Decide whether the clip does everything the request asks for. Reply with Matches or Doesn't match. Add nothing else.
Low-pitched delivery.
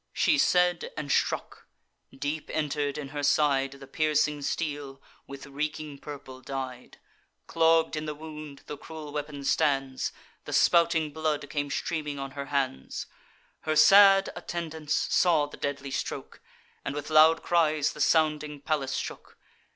Doesn't match